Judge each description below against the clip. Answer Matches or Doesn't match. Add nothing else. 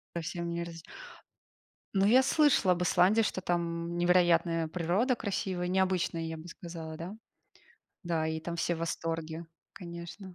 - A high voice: Doesn't match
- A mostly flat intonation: Matches